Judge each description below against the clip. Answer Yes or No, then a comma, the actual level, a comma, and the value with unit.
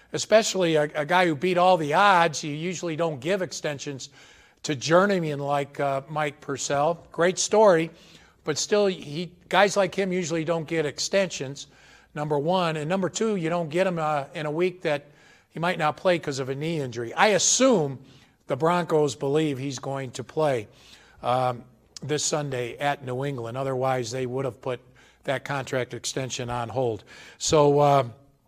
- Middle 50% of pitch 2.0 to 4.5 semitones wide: Yes, average, 4.2 semitones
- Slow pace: No, average, 175 wpm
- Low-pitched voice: No, medium, 150 Hz